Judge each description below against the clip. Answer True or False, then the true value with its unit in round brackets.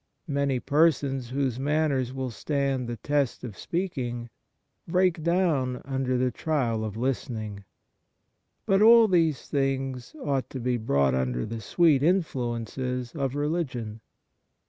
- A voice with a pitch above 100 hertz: True (135 Hz)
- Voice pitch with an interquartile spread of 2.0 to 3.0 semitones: False (4.1 semitones)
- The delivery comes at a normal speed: False (130 wpm)